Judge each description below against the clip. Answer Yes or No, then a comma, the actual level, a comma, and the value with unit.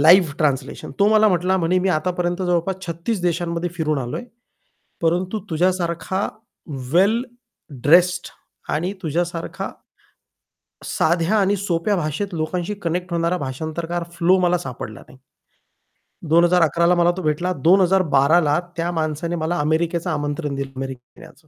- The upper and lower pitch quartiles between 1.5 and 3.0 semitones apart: Yes, narrow, 2.5 semitones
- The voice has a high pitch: No, medium, 170 Hz